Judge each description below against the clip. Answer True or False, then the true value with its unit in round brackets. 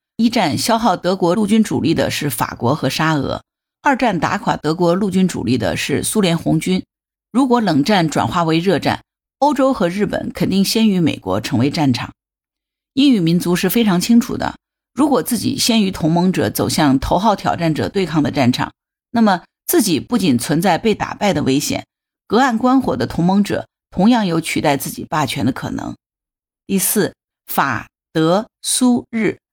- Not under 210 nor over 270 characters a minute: True (260 characters per minute)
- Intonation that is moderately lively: False (6.7 semitones)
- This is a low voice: False (185 Hz)